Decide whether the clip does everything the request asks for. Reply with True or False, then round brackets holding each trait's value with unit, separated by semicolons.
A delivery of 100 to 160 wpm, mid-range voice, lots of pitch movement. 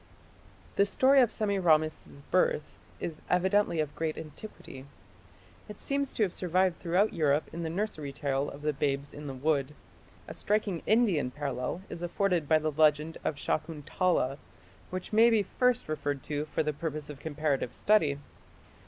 False (155 wpm; 160 Hz; 4.6 semitones)